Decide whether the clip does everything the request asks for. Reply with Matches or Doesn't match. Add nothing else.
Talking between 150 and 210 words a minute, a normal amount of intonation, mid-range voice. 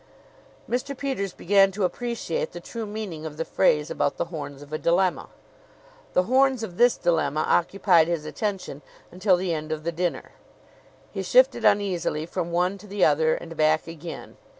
Matches